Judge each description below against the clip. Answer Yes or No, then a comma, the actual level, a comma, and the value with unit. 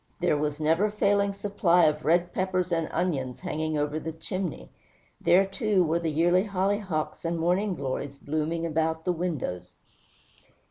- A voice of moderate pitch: Yes, medium, 170 Hz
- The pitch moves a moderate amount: Yes, average, 3.3 semitones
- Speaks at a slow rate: No, average, 155 wpm